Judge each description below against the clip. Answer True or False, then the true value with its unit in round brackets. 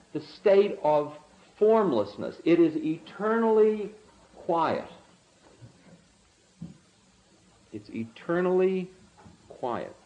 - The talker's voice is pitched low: False (200 Hz)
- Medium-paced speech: False (65 wpm)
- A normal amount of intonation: True (4.0 semitones)